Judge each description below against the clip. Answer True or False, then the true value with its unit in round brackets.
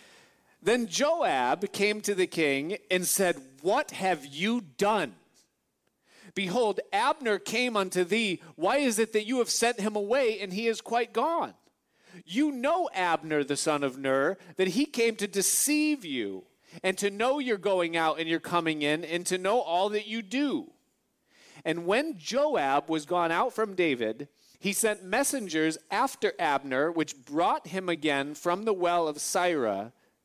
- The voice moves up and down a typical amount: False (5.7 semitones)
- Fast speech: False (165 wpm)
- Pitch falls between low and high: False (195 Hz)